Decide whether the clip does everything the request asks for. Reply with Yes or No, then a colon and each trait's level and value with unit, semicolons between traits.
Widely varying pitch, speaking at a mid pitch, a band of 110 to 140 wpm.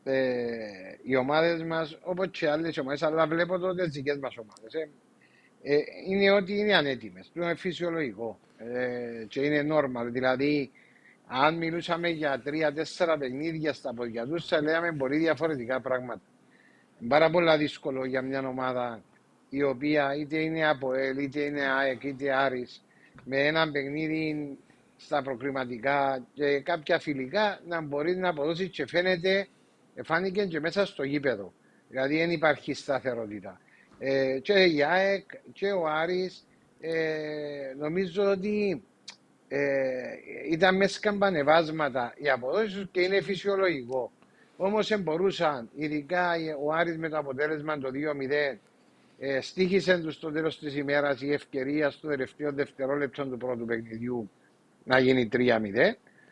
No: average, 4.2 semitones; medium, 150 Hz; average, 135 wpm